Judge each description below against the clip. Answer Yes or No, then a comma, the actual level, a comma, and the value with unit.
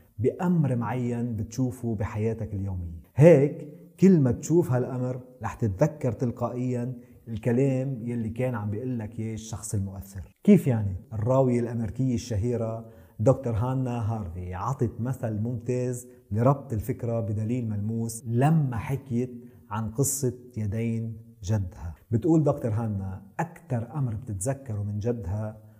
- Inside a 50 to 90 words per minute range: No, average, 115 wpm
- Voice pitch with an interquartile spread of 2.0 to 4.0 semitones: Yes, average, 2.9 semitones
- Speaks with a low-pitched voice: Yes, low, 120 Hz